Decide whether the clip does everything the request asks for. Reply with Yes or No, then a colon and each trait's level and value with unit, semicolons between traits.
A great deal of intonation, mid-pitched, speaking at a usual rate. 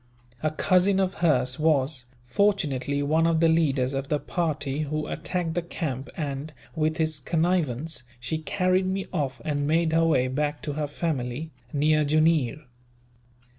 No: average, 2.7 semitones; medium, 155 Hz; average, 155 wpm